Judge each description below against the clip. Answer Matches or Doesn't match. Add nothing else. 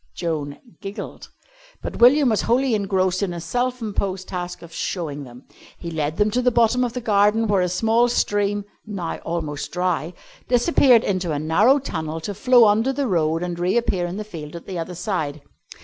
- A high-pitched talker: Matches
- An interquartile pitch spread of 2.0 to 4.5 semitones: Doesn't match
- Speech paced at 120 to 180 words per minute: Doesn't match